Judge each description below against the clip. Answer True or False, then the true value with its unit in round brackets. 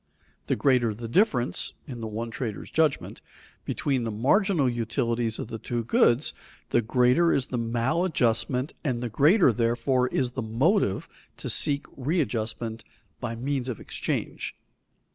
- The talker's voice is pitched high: False (125 Hz)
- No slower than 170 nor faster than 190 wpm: False (145 wpm)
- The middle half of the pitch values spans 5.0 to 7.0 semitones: False (3.2 semitones)